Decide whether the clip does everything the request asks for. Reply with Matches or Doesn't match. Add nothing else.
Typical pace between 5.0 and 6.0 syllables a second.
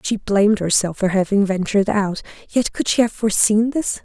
Matches